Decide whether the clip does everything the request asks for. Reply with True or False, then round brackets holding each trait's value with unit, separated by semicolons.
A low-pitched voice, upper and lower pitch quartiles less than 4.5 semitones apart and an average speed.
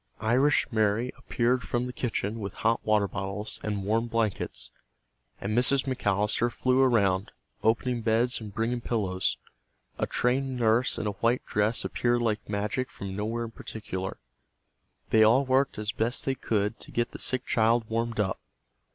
True (115 Hz; 2.7 semitones; 160 wpm)